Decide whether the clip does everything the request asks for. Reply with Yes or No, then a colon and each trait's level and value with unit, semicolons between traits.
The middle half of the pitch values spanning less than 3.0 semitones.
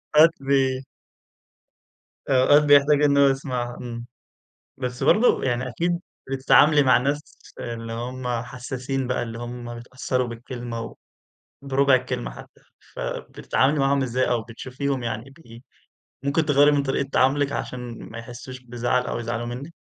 Yes: narrow, 2.5 semitones